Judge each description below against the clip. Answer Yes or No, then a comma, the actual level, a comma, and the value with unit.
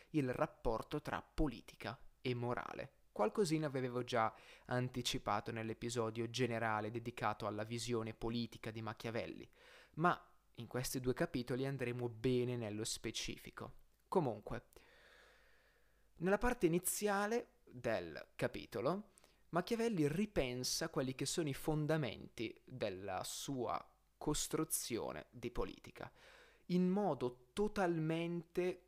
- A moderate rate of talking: No, slow, 100 wpm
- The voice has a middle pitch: No, low, 130 Hz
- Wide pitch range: Yes, wide, 6.6 semitones